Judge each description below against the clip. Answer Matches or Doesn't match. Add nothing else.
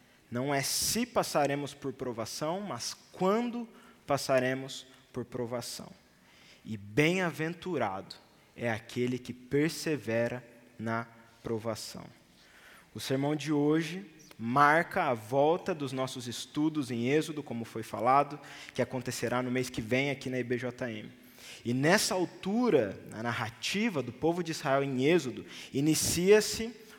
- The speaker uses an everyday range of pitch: Matches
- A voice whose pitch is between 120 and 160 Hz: Matches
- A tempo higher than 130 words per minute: Doesn't match